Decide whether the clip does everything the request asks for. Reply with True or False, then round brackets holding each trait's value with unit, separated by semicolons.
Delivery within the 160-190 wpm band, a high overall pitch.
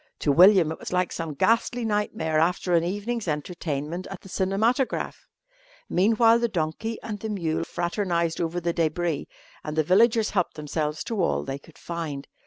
False (170 wpm; 175 Hz)